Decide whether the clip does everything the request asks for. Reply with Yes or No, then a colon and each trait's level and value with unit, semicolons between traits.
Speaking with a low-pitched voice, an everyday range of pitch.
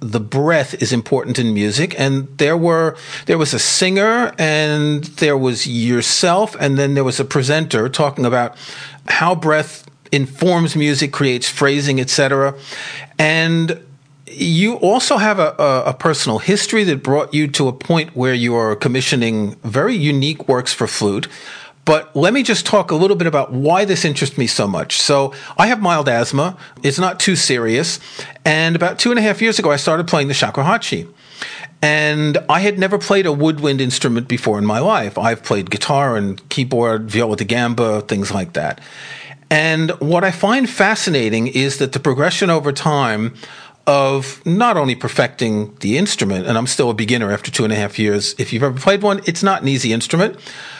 No: medium, 145 Hz; average, 4.7 semitones